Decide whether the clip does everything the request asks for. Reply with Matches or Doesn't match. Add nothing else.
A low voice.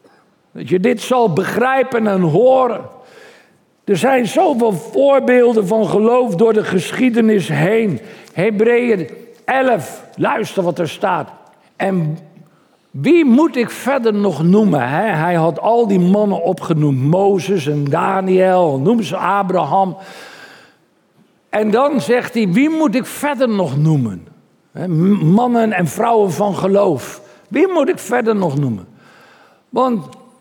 Doesn't match